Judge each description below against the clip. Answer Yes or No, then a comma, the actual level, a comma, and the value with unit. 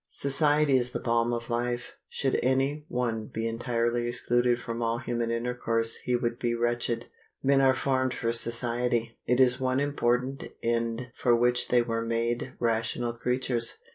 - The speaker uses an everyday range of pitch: No, narrow, 1.4 semitones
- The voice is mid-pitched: No, low, 120 Hz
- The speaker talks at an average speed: Yes, average, 160 wpm